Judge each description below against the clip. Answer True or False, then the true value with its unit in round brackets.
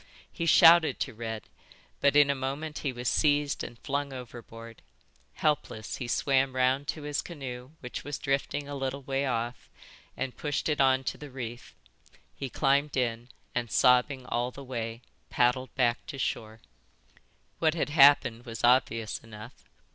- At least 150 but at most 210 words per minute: True (160 wpm)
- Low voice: True (130 Hz)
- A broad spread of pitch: False (2.9 semitones)